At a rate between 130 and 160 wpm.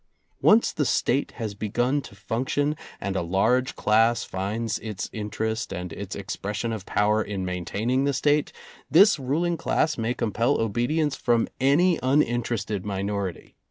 Yes: average, 155 wpm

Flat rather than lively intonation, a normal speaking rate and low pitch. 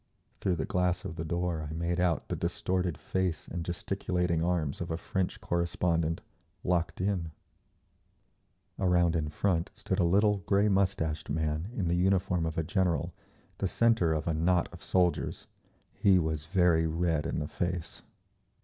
Yes: narrow, 2.0 semitones; average, 160 wpm; very low, 85 Hz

